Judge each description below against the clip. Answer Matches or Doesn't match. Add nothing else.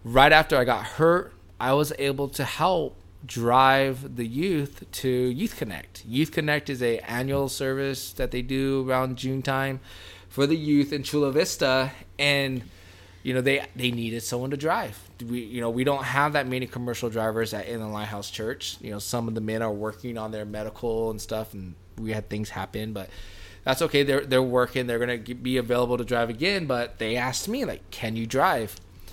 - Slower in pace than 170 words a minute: Doesn't match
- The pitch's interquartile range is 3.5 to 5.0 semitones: Matches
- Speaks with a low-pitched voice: Matches